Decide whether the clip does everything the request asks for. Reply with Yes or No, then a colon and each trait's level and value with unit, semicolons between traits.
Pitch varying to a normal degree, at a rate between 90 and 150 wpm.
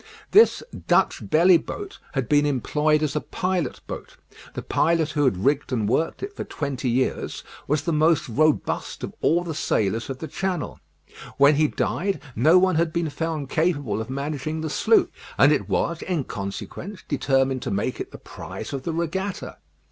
No: average, 4.0 semitones; average, 180 wpm